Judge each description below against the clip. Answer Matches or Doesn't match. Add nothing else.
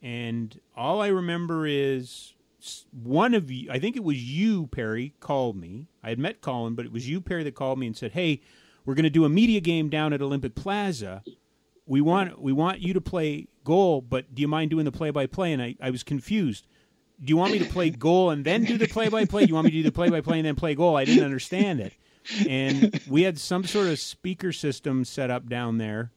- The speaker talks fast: Matches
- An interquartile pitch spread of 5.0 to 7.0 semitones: Matches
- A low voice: Doesn't match